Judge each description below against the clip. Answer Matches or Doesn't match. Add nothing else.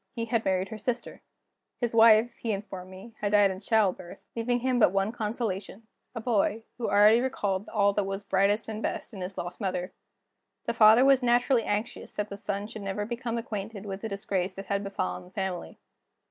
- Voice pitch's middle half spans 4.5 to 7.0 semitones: Doesn't match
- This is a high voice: Matches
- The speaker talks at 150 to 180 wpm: Doesn't match